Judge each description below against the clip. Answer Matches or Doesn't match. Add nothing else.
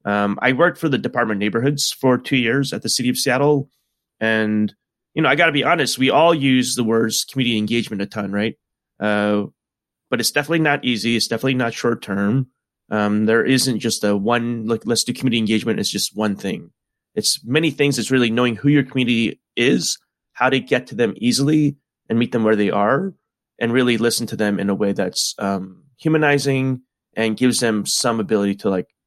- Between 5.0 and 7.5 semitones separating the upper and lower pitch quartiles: Doesn't match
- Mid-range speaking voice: Doesn't match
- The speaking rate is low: Doesn't match